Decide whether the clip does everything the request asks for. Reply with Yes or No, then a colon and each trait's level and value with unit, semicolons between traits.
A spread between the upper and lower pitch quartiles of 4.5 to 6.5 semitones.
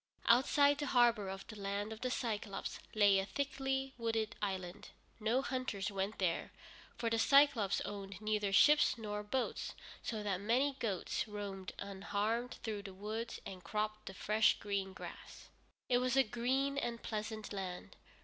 No: average, 3.4 semitones